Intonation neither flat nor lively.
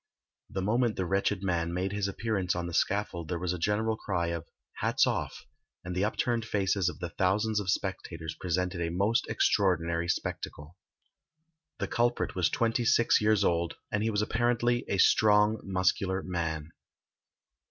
Yes: average, 3.6 semitones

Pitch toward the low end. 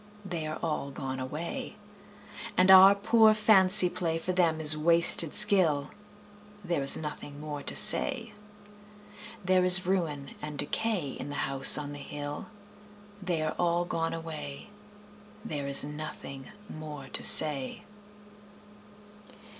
No: medium, 160 Hz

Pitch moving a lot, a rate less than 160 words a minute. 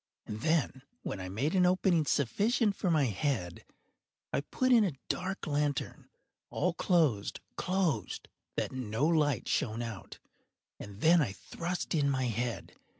Yes: wide, 7.0 semitones; average, 150 wpm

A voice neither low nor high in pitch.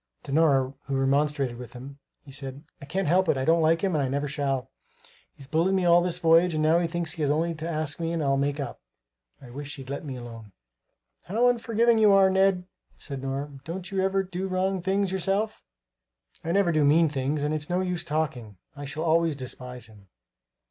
Yes: medium, 155 Hz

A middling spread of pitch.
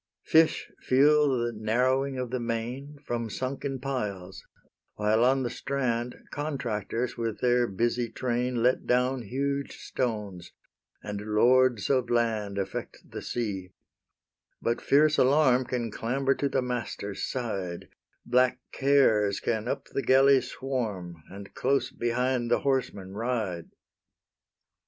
Yes: average, 3.4 semitones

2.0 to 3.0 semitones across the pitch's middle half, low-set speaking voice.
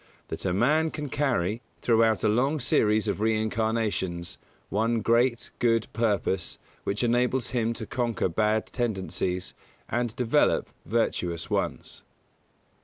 Yes: narrow, 2.5 semitones; low, 115 Hz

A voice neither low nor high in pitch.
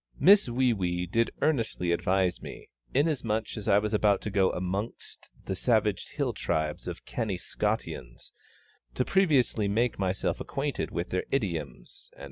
No: low, 105 Hz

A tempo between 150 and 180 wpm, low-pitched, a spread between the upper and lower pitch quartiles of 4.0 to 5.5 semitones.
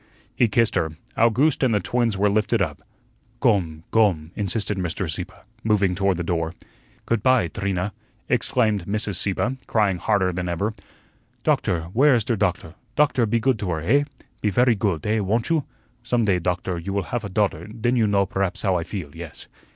No: average, 190 wpm; low, 100 Hz; average, 4.3 semitones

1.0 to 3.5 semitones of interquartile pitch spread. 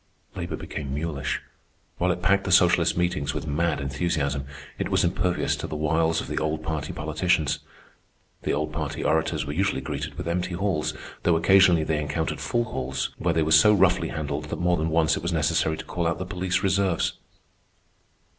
Yes: average, 2.7 semitones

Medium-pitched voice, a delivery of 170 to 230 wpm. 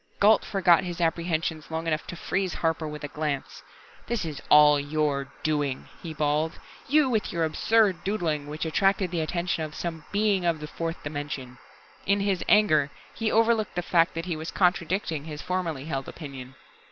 Yes: medium, 165 Hz; average, 175 wpm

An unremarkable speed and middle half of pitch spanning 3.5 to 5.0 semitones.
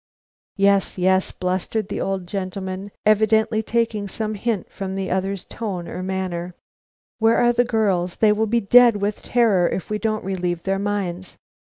No: average, 170 wpm; narrow, 2.6 semitones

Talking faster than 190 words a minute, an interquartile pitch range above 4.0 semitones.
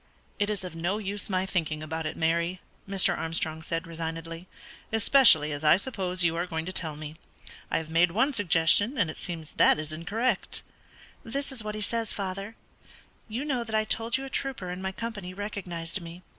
Yes: average, 200 wpm; average, 4.6 semitones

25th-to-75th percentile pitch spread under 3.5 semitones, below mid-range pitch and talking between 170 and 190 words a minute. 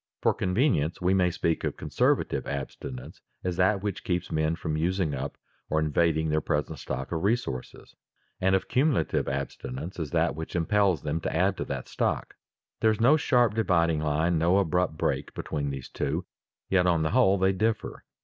No: average, 3.8 semitones; very low, 85 Hz; average, 180 wpm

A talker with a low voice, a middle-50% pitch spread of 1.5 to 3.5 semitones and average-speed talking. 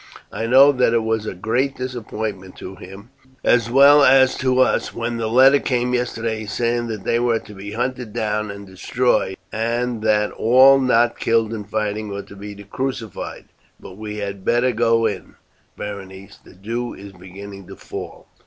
Yes: low, 115 Hz; average, 3.2 semitones; average, 175 wpm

